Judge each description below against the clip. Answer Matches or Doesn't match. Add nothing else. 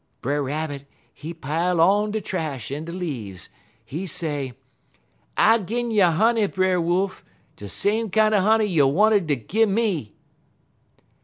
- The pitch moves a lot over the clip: Matches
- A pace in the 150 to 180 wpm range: Doesn't match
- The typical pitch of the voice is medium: Matches